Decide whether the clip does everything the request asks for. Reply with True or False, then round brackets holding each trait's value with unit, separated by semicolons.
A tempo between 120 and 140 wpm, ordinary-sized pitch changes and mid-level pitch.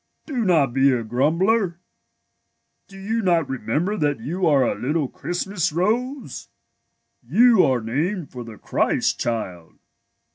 False (135 wpm; 6.9 semitones; 165 Hz)